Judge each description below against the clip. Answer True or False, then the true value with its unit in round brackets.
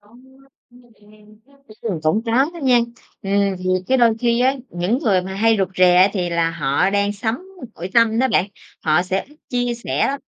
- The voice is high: True (215 Hz)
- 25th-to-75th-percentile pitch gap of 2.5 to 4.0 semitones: False (4.5 semitones)